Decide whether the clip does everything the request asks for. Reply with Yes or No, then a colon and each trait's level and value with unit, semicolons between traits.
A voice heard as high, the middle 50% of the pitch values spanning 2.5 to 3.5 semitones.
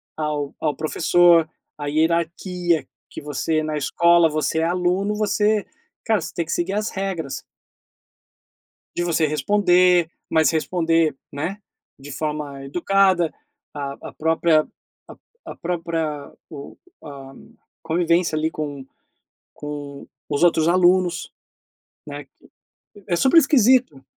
No: medium, 165 Hz; average, 2.9 semitones